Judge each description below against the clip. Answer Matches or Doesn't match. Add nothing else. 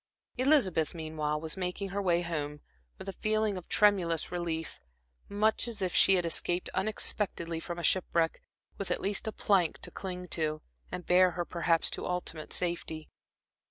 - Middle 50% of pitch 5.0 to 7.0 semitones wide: Doesn't match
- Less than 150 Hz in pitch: Doesn't match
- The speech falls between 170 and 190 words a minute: Doesn't match